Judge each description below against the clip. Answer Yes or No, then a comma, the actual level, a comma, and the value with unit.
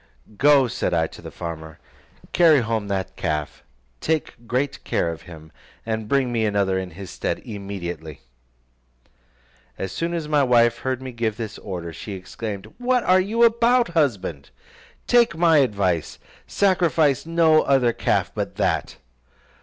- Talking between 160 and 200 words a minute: No, average, 150 wpm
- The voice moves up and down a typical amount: No, wide, 8.9 semitones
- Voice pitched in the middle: No, low, 115 Hz